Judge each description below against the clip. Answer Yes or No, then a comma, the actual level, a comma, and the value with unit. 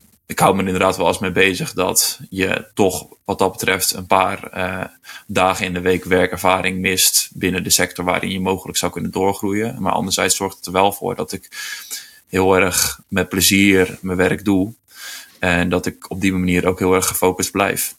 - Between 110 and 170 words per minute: No, average, 195 wpm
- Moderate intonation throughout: No, narrow, 1.3 semitones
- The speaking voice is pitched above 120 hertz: No, very low, 95 Hz